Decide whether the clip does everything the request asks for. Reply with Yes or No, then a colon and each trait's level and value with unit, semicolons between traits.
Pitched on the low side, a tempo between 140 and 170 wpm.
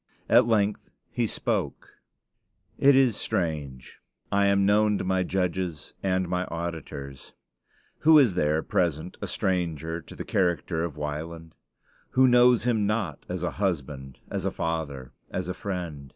Yes: very low, 90 Hz; average, 150 wpm